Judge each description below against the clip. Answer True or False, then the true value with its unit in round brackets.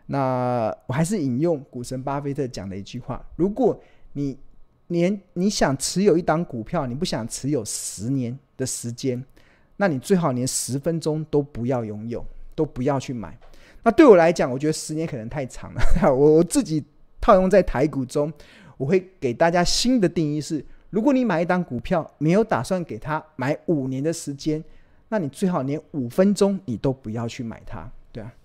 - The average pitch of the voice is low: False (145 Hz)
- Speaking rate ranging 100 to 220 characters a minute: False (270 characters per minute)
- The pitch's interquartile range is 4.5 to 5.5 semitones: True (5.2 semitones)